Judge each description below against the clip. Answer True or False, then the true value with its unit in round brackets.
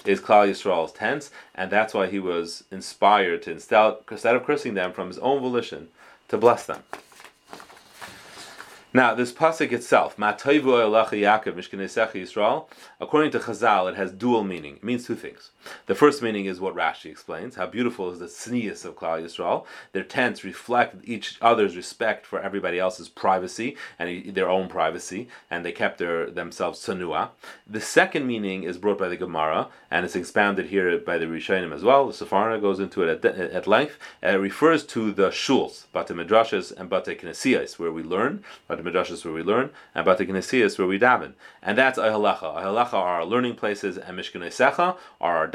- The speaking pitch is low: True (105 Hz)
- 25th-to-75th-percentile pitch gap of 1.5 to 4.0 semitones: False (5.1 semitones)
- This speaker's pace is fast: False (180 wpm)